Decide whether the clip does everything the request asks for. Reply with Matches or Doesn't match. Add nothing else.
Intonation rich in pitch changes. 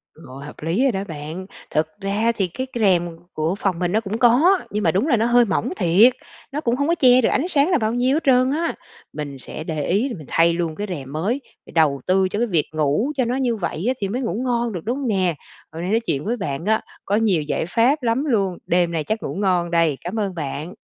Matches